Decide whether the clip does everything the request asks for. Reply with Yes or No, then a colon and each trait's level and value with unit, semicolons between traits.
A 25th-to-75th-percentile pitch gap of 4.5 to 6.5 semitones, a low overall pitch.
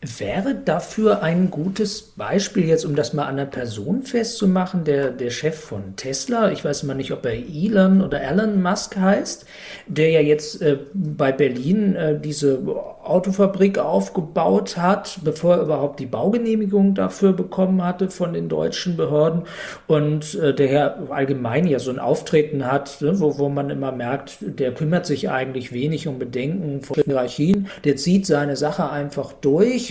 No: wide, 5.5 semitones; medium, 155 Hz